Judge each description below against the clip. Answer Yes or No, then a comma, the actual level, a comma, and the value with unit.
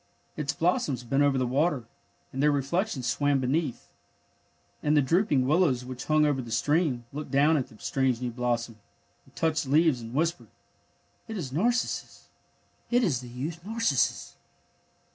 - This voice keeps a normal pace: Yes, average, 165 wpm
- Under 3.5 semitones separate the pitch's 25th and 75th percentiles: No, average, 4.2 semitones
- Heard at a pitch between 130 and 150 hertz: Yes, medium, 140 Hz